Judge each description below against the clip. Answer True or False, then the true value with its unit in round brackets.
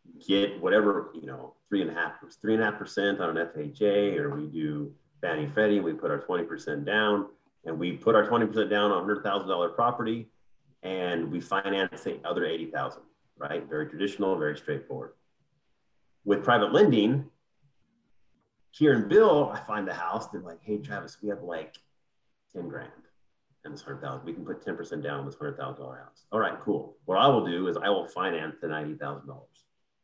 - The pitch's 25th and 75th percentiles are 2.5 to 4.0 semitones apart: False (4.7 semitones)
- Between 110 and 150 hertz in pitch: False (100 Hz)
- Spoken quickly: False (185 wpm)